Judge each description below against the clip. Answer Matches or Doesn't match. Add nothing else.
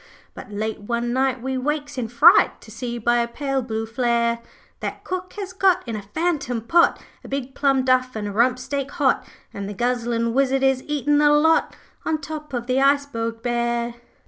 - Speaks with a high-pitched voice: Matches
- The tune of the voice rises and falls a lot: Doesn't match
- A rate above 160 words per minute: Matches